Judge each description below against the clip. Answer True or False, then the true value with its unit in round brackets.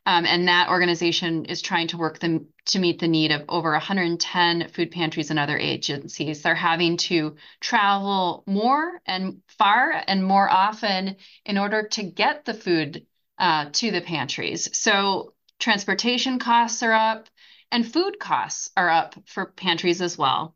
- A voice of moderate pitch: True (175 Hz)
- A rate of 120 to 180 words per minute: True (160 wpm)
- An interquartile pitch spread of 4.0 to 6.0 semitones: False (3.5 semitones)